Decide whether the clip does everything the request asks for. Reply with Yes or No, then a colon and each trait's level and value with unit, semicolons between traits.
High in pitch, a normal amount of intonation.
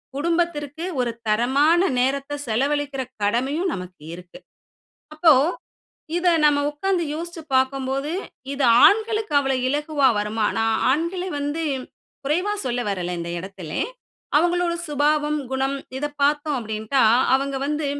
Yes: very high, 285 Hz; average, 4.0 semitones